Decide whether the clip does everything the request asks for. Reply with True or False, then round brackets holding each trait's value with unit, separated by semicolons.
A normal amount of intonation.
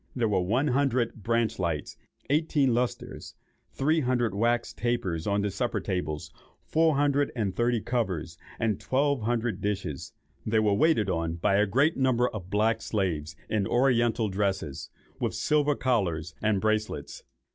True (4.5 semitones)